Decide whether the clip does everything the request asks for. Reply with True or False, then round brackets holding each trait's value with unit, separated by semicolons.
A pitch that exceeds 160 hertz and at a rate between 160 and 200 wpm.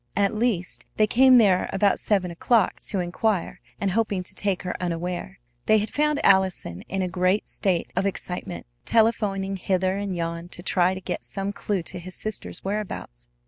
True (190 Hz; 180 wpm)